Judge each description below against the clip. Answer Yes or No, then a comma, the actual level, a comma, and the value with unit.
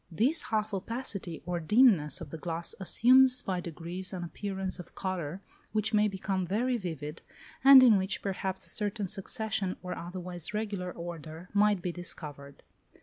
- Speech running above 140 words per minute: Yes, average, 155 wpm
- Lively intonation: No, average, 3.5 semitones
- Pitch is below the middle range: No, high, 190 Hz